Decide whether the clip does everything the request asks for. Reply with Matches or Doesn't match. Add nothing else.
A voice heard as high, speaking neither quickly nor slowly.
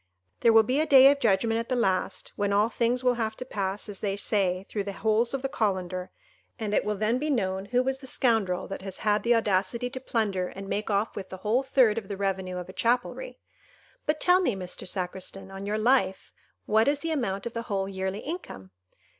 Doesn't match